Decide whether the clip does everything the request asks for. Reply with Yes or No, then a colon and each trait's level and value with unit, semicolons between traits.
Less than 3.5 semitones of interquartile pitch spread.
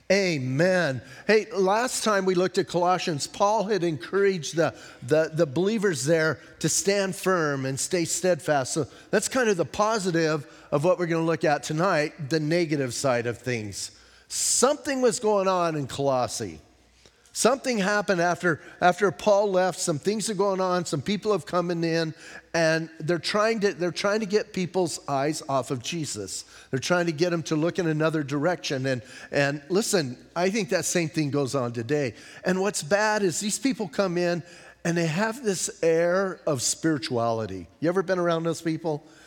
No: average, 4.3 semitones